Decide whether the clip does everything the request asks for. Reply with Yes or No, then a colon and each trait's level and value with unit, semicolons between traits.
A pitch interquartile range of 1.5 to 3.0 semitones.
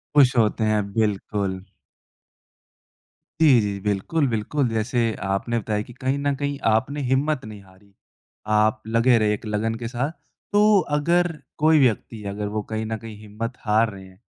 No: average, 3.9 semitones